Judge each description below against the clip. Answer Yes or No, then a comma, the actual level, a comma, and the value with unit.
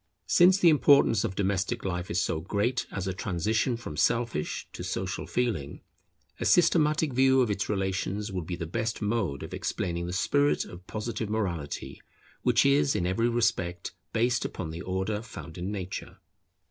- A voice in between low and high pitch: No, low, 100 Hz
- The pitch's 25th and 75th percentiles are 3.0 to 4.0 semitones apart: No, average, 4.9 semitones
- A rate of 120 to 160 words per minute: No, average, 170 wpm